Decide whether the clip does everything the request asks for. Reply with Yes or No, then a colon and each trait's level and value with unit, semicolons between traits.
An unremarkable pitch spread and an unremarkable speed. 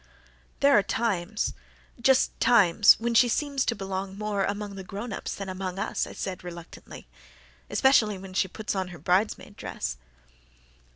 Yes: average, 3.0 semitones; average, 160 wpm